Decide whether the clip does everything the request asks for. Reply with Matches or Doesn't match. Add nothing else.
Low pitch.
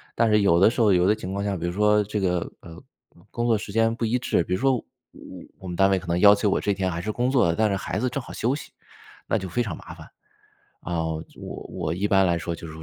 Matches